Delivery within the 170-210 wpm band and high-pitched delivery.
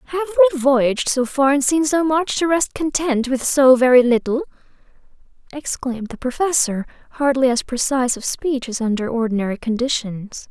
No: average, 160 wpm; very high, 265 Hz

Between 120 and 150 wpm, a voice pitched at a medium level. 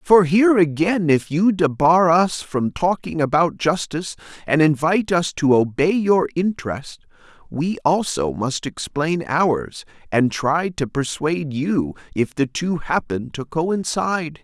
Yes: average, 140 wpm; medium, 160 Hz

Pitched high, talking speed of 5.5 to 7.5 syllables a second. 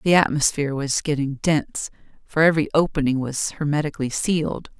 No: medium, 150 Hz; 5.9 syllables/s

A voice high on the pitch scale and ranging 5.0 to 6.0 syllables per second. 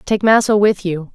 No: high, 200 Hz; 4.8 syllables/s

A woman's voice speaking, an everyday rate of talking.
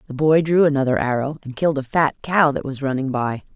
No: female; fast, 235 wpm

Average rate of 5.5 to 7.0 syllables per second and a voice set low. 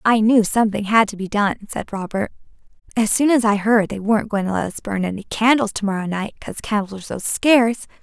No: 6.0 syllables/s; high, 210 Hz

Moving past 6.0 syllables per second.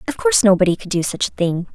Yes: 7.1 syllables/s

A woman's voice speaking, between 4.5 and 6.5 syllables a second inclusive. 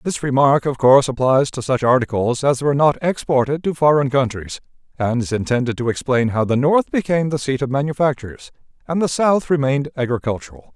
No: male; 5.9 syllables/s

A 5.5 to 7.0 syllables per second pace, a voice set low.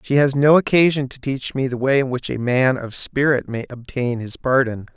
No: 5.0 syllables/s; low, 130 Hz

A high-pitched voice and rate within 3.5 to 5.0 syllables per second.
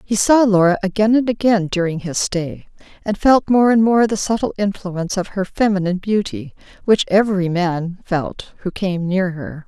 Yes: high, 195 Hz; 4.9 syllables/s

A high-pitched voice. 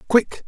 Yes: high, 235 Hz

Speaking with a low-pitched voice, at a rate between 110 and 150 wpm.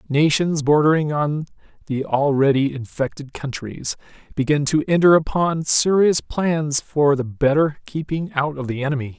No: medium, 145 Hz; slow, 135 wpm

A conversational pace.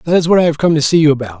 No: fast, 430 wpm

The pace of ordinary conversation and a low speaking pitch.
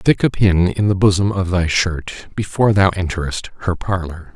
Yes: average, 195 wpm; very low, 95 Hz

